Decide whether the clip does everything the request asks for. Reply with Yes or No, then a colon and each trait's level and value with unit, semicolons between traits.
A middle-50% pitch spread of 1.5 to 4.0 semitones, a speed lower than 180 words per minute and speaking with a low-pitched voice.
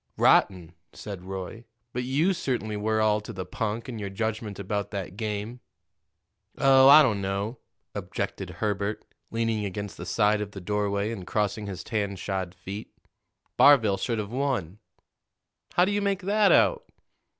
Yes: average, 3.1 semitones; average, 160 wpm; low, 105 Hz